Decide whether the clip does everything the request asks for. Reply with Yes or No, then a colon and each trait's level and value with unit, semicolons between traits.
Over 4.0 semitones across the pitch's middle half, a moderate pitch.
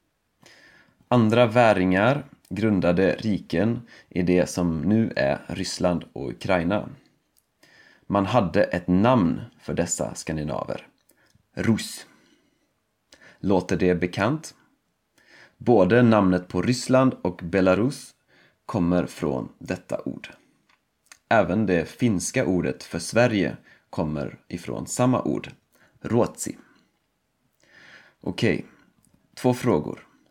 No: wide, 5.4 semitones; very low, 95 Hz